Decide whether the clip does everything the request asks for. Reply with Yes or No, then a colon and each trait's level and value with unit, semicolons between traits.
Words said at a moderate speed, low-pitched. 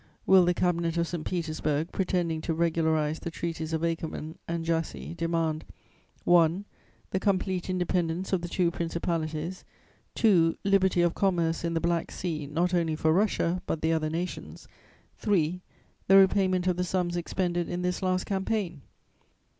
No: average, 155 wpm; medium, 170 Hz